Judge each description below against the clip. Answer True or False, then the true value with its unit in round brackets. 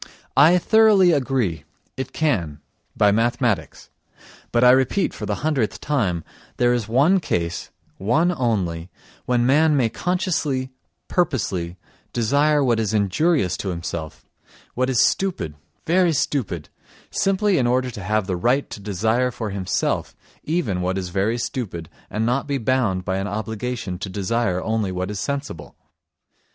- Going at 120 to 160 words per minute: True (145 wpm)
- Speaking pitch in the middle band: False (120 Hz)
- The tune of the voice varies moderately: False (6.7 semitones)